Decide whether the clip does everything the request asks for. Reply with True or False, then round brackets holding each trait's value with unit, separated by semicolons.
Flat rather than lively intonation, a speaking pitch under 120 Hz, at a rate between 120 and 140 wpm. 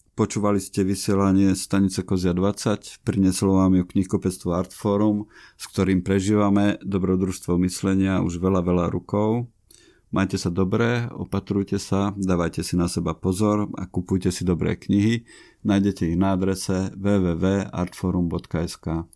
True (1.8 semitones; 95 Hz; 125 wpm)